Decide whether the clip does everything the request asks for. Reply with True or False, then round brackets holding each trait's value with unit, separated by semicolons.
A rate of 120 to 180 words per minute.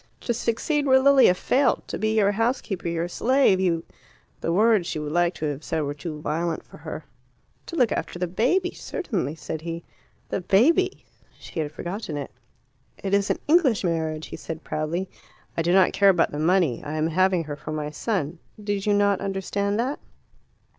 False (195 wpm)